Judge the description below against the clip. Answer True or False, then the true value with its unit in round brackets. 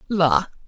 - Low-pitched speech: False (180 Hz)